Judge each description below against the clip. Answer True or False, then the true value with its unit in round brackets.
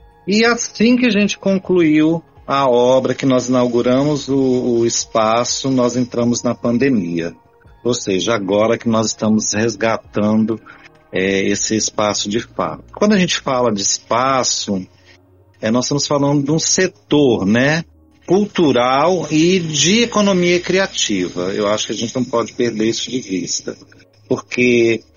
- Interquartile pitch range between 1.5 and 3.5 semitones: False (5.5 semitones)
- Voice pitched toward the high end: False (120 Hz)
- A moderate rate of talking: True (145 wpm)